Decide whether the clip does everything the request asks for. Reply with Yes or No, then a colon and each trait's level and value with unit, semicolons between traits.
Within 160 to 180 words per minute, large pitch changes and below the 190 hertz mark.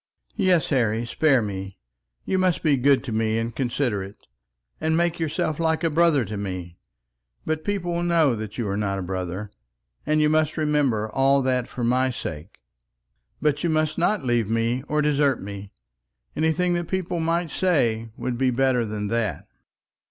Yes: average, 170 wpm; wide, 6.3 semitones; low, 135 Hz